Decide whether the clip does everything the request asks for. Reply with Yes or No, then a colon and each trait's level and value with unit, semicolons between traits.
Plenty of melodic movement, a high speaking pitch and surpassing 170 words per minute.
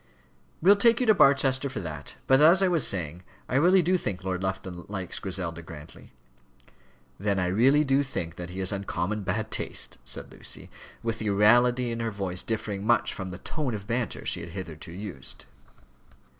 No: wide, 6.4 semitones; low, 105 Hz; average, 185 wpm